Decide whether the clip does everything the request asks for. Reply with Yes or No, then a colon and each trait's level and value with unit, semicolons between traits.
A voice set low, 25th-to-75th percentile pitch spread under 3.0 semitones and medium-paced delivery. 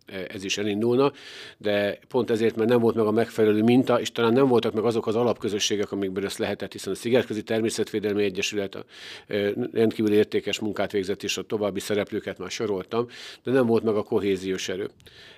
No: low, 110 Hz; narrow, 2.4 semitones; fast, 185 wpm